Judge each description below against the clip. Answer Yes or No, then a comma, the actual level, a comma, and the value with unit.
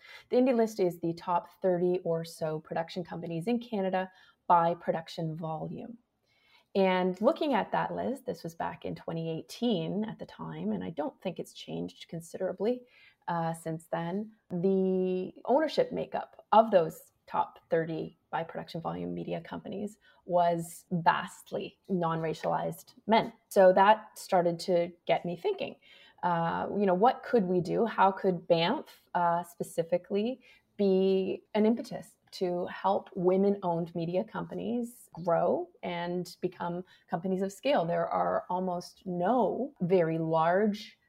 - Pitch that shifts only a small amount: No, average, 3.8 semitones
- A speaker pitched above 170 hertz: Yes, medium, 185 Hz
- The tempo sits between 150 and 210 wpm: No, average, 140 wpm